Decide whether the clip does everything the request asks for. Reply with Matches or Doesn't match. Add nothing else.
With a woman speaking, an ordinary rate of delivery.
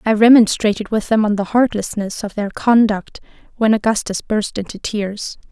Matches